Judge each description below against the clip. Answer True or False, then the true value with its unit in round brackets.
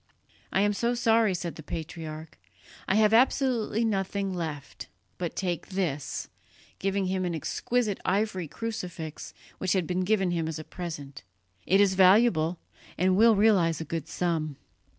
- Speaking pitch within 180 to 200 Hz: True (185 Hz)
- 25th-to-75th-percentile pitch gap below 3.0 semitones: False (4.0 semitones)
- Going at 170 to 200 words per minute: False (150 wpm)